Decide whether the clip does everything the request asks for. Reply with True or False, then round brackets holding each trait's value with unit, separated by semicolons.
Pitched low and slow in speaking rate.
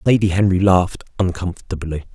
True (90 Hz; 110 wpm)